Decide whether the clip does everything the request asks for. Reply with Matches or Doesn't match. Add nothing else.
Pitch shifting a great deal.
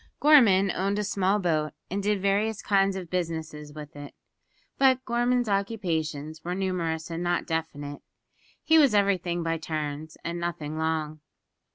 Doesn't match